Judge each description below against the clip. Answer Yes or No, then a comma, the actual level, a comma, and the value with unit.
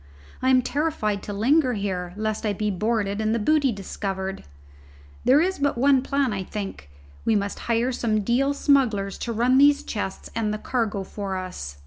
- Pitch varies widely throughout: No, average, 4.6 semitones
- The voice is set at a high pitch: Yes, high, 220 Hz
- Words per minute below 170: No, average, 180 wpm